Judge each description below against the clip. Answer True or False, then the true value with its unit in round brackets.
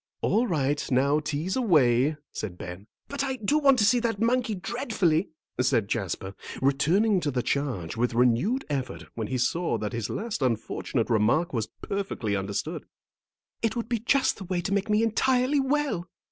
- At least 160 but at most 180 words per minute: True (175 wpm)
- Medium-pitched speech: True (165 Hz)